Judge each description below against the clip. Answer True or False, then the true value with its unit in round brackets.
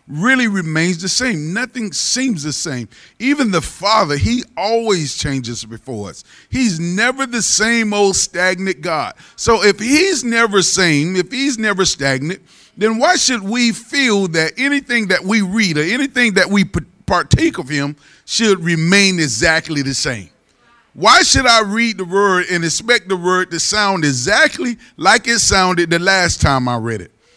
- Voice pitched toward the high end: True (195 Hz)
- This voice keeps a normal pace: True (165 wpm)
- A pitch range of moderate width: False (6.1 semitones)